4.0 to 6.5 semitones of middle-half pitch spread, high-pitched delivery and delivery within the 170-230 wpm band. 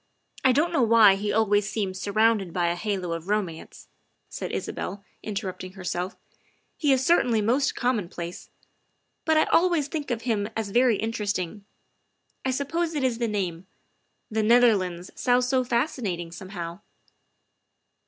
No: average, 5.1 semitones; high, 215 Hz; average, 155 wpm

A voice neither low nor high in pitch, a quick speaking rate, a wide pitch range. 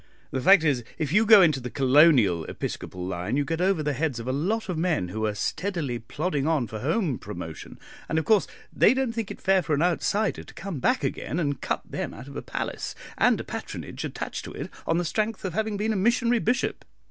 Yes: medium, 160 Hz; fast, 230 wpm; wide, 7.0 semitones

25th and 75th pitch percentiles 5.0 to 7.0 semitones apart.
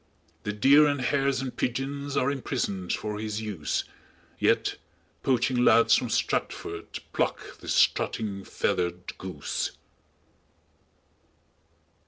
Yes: wide, 5.5 semitones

